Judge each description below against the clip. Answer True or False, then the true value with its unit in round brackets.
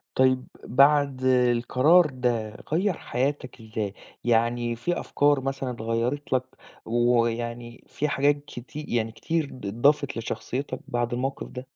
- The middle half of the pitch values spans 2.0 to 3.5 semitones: True (3.0 semitones)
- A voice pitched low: True (125 Hz)